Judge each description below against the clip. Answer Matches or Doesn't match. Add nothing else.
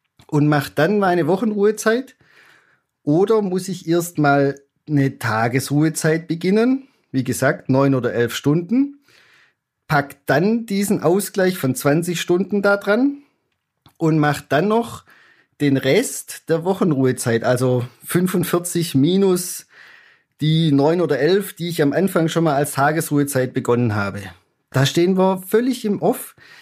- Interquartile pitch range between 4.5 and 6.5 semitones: Matches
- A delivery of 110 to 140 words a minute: Matches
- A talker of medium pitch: Matches